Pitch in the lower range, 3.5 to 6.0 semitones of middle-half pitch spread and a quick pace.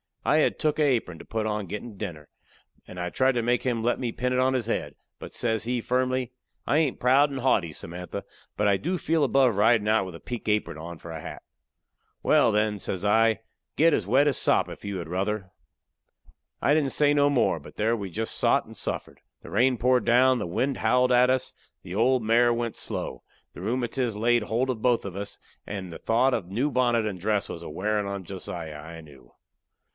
Yes: low, 115 Hz; average, 4.6 semitones; fast, 225 wpm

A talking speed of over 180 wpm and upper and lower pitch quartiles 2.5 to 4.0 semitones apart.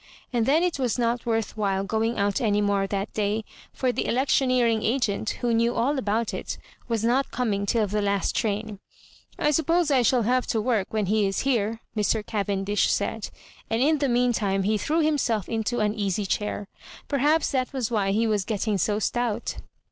Yes: average, 200 wpm; average, 3.3 semitones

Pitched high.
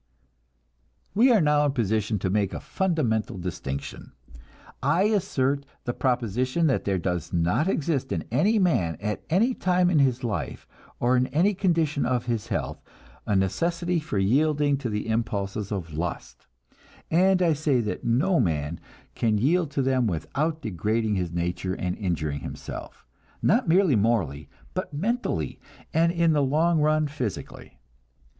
No: low, 130 Hz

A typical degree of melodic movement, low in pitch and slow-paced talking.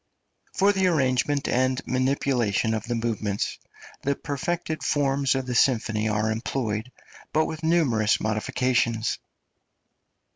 Yes: average, 4.2 semitones; low, 130 Hz; slow, 115 wpm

